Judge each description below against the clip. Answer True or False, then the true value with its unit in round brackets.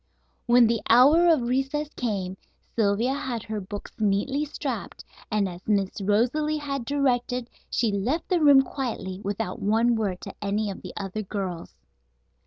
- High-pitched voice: True (230 Hz)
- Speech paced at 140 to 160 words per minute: True (155 wpm)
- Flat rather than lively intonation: False (5.1 semitones)